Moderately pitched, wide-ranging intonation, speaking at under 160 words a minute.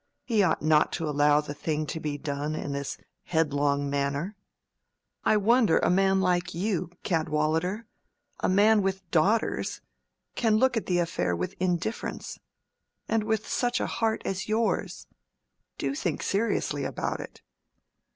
Yes: medium, 175 Hz; wide, 5.9 semitones; average, 140 wpm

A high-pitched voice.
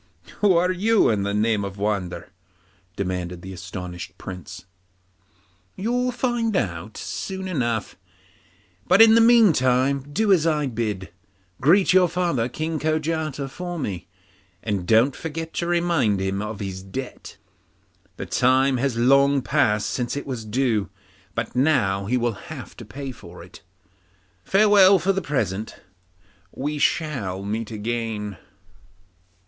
No: low, 130 Hz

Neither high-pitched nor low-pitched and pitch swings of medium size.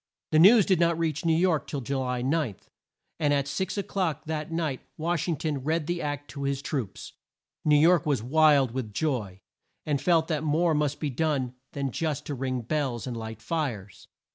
Yes: medium, 150 Hz; average, 3.5 semitones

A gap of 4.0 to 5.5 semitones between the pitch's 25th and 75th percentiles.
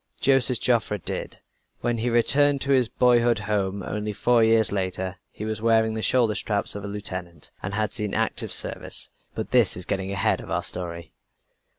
No: average, 3.2 semitones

